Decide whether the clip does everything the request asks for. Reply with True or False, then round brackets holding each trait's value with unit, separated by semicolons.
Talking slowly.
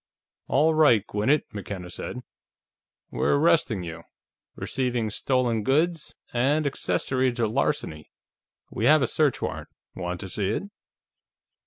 True (125 wpm)